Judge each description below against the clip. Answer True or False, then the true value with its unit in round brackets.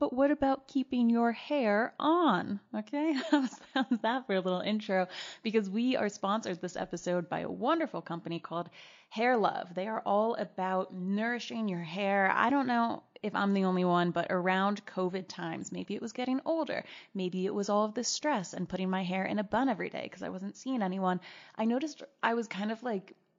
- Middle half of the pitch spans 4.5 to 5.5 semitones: True (5.1 semitones)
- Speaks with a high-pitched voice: True (210 Hz)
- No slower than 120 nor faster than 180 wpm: False (205 wpm)